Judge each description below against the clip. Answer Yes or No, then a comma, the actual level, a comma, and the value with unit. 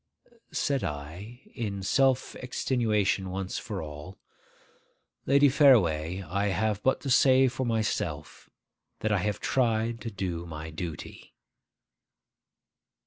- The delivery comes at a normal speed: No, slow, 115 wpm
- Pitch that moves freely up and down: Yes, wide, 5.8 semitones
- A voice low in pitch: Yes, low, 105 Hz